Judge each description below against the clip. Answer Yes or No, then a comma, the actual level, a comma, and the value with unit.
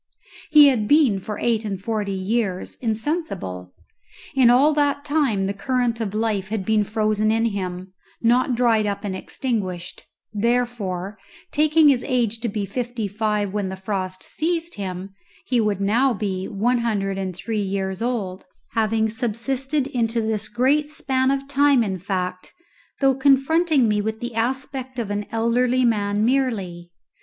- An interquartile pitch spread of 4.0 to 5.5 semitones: Yes, average, 4.3 semitones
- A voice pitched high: Yes, high, 225 Hz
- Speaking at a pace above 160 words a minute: No, average, 155 wpm